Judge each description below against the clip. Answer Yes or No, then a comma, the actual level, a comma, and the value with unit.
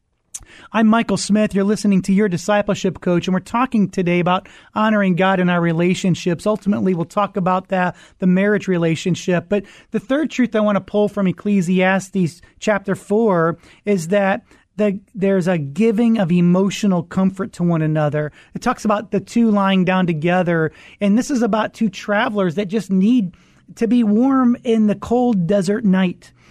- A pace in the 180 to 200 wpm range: No, average, 170 wpm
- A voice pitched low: No, high, 195 Hz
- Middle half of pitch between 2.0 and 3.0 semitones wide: Yes, average, 2.7 semitones